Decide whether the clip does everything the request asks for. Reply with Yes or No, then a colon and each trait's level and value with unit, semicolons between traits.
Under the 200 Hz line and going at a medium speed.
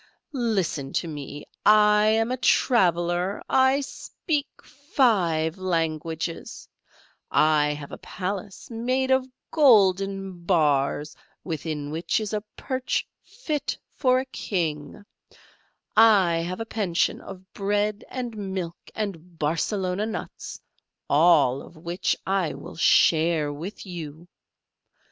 No: medium, 185 Hz; slow, 110 wpm